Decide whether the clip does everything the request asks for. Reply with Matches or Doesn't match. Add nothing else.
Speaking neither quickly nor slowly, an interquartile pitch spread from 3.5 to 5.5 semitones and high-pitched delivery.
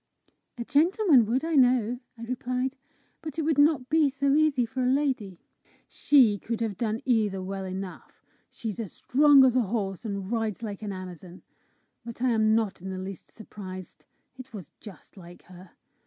Matches